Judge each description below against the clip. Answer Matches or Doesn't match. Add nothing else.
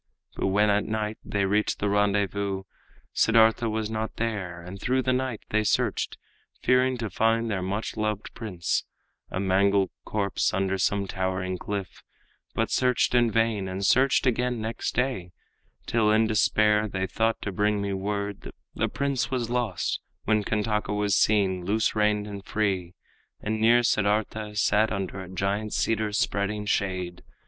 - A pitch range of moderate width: Doesn't match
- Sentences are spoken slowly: Doesn't match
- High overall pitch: Doesn't match